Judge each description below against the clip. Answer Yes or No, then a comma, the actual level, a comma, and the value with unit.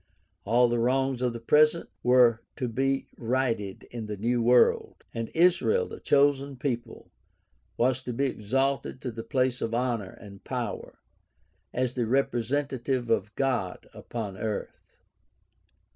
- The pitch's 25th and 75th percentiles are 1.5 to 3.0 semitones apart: Yes, narrow, 2.6 semitones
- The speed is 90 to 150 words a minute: Yes, average, 140 wpm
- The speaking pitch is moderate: No, low, 125 Hz